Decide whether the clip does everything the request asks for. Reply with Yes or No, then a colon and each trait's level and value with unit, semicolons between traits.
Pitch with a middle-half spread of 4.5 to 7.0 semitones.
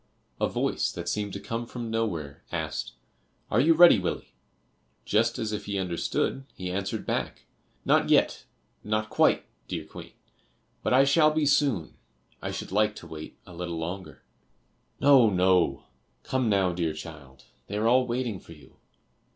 Yes: wide, 5.4 semitones